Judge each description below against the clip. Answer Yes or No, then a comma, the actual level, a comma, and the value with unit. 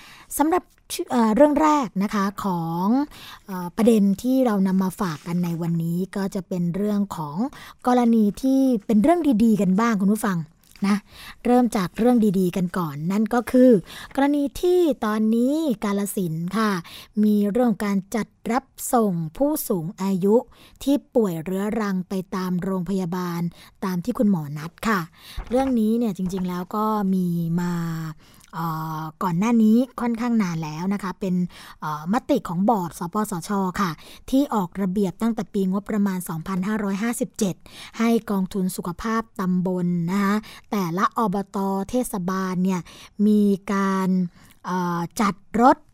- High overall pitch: Yes, high, 200 Hz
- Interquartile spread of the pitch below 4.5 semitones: Yes, average, 4.1 semitones